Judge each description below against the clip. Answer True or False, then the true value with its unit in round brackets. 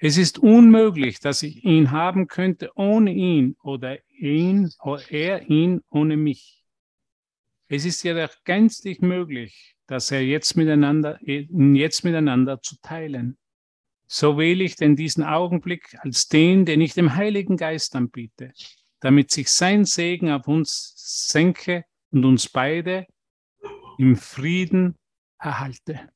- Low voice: False (155 Hz)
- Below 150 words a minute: True (130 wpm)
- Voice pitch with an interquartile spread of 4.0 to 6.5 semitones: True (4.4 semitones)